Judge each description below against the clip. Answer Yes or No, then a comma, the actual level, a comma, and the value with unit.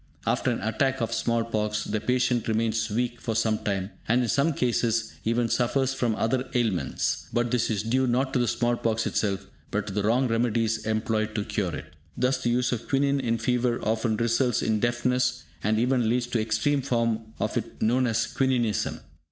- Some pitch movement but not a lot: No, narrow, 2.2 semitones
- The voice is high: No, low, 115 Hz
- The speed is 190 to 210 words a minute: Yes, average, 195 wpm